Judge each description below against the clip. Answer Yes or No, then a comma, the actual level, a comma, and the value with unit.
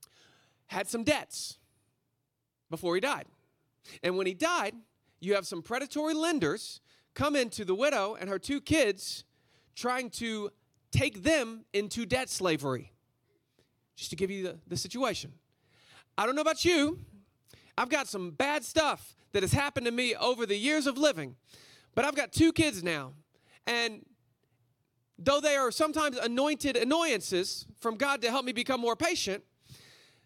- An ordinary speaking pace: Yes, average, 155 wpm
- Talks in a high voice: Yes, high, 225 Hz